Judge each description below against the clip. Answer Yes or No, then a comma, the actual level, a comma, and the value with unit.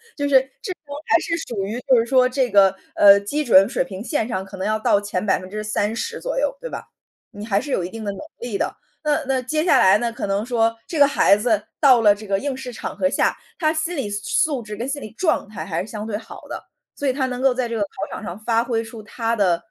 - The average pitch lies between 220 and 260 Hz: Yes, high, 230 Hz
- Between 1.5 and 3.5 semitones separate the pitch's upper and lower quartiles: No, average, 4.8 semitones